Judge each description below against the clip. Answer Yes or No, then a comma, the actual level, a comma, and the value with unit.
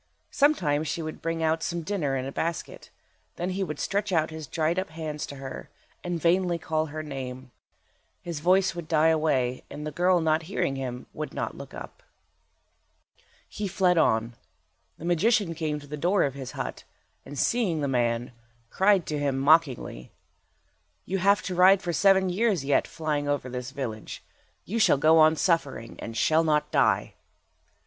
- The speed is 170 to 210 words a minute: Yes, average, 175 wpm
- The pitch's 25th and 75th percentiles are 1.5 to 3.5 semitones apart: No, average, 4.0 semitones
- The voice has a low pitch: No, medium, 160 Hz